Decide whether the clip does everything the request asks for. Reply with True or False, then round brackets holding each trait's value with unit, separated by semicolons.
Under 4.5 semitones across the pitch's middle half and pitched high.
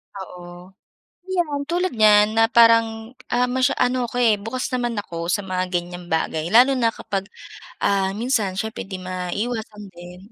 False (4.8 semitones; 215 Hz)